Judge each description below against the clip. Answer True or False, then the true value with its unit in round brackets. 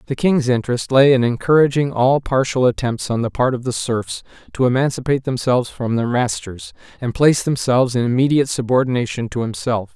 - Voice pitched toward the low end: True (125 Hz)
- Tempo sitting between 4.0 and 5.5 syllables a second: False (5.9 syllables/s)